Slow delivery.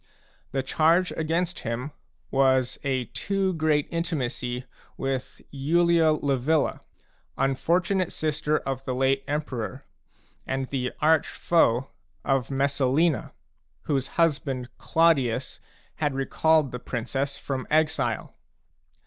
Yes: slow, 105 wpm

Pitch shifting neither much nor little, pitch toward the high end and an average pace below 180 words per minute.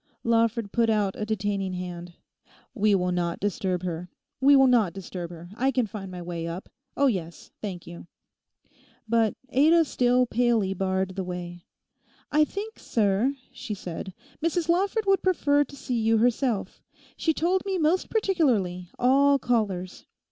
No: wide, 7.0 semitones; high, 220 Hz; average, 155 wpm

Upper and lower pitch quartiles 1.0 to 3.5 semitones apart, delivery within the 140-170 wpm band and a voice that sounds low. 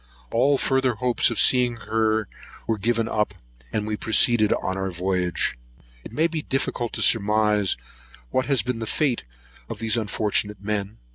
Yes: average, 2.7 semitones; average, 160 wpm; low, 110 Hz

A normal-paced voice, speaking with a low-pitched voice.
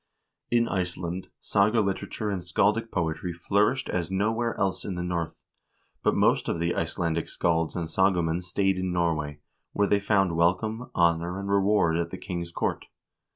Yes: average, 160 wpm; very low, 90 Hz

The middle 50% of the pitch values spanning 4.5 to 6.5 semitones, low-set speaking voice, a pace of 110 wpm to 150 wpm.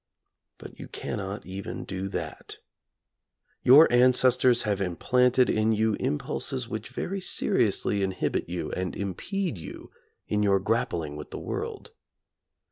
Yes: average, 5.0 semitones; low, 105 Hz; slow, 135 wpm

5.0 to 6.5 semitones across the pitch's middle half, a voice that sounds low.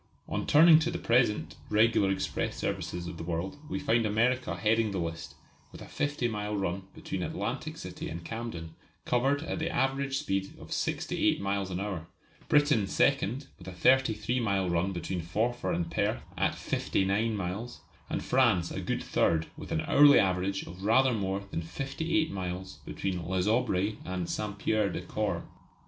Yes: average, 5.3 semitones; low, 105 Hz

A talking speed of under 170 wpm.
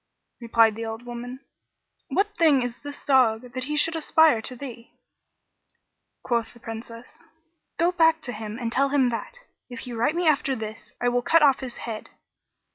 No: average, 180 wpm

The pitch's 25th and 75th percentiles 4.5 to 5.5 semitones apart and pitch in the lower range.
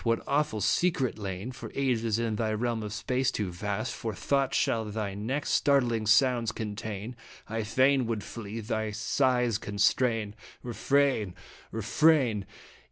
No: average, 3.3 semitones; low, 115 Hz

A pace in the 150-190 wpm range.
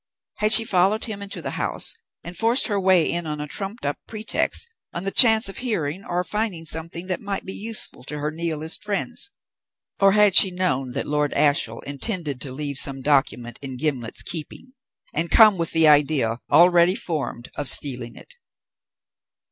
Yes: average, 180 wpm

